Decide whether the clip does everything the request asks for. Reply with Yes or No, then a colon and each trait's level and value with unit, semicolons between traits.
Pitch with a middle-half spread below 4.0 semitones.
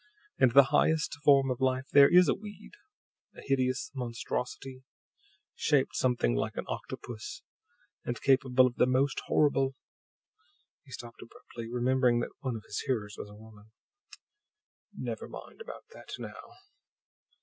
Yes: average, 2.7 semitones